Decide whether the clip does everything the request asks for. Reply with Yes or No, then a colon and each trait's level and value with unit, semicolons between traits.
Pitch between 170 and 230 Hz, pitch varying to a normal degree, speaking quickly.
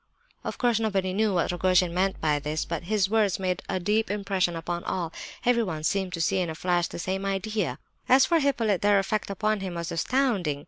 Yes: high, 190 Hz; average, 3.5 semitones; fast, 210 wpm